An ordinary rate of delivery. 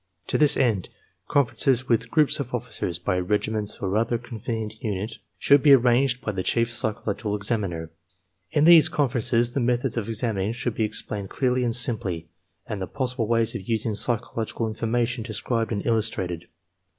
Yes: average, 170 wpm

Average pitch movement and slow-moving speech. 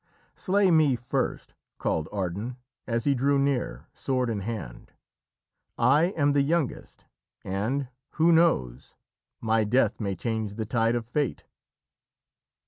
Yes: average, 4.8 semitones; slow, 130 wpm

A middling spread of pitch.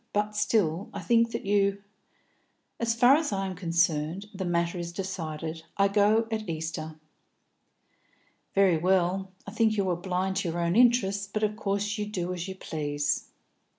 Yes: average, 3.5 semitones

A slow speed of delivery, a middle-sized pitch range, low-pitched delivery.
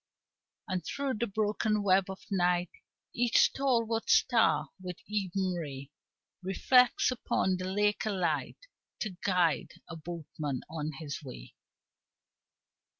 No: slow, 120 wpm; average, 4.4 semitones; medium, 185 Hz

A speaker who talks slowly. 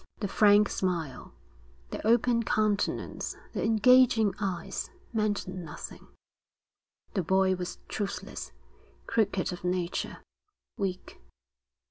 Yes: slow, 95 wpm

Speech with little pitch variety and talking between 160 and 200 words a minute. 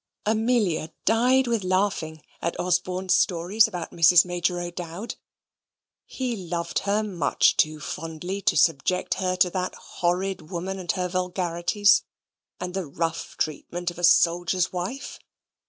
No: narrow, 2.2 semitones; slow, 135 wpm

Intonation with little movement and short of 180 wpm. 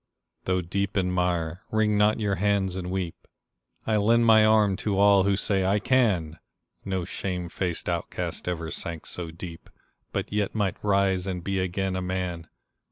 Yes: narrow, 2.3 semitones; average, 170 wpm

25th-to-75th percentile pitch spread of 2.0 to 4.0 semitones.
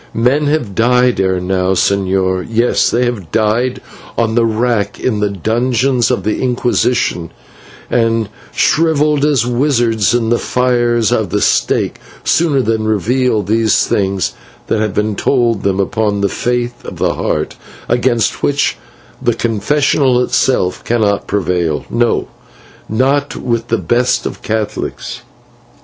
Yes: average, 3.3 semitones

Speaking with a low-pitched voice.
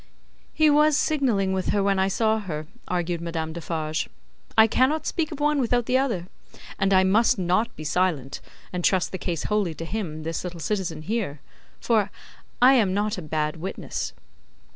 No: high, 190 Hz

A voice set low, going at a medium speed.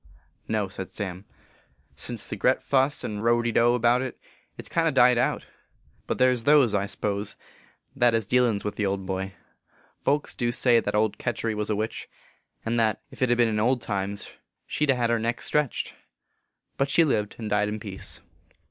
No: low, 115 Hz; fast, 210 wpm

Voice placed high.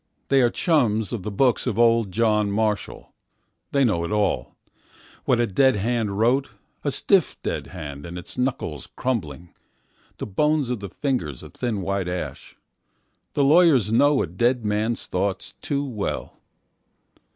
No: low, 110 Hz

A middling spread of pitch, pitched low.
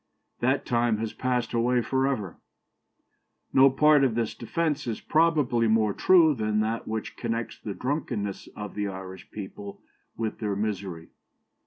Yes: average, 4.1 semitones; low, 115 Hz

